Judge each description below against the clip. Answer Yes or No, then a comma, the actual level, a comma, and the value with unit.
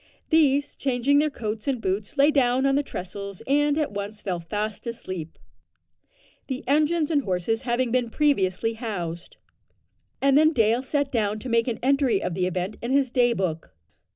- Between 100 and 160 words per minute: No, average, 175 wpm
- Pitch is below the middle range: No, high, 240 Hz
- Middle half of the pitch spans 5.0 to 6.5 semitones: Yes, wide, 5.5 semitones